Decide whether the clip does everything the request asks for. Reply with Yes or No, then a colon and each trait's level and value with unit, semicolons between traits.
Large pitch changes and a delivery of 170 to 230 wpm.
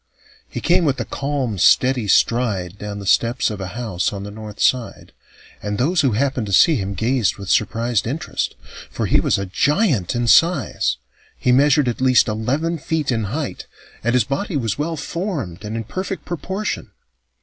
Yes: wide, 5.8 semitones; average, 185 wpm